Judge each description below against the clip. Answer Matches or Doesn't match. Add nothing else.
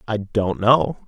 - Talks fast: Doesn't match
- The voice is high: Doesn't match